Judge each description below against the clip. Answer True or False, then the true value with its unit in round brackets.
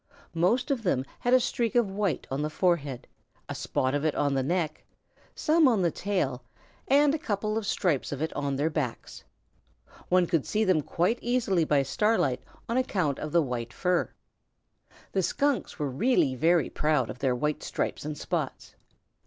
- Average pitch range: False (7.2 semitones)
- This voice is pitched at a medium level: True (170 Hz)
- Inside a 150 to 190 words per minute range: True (180 wpm)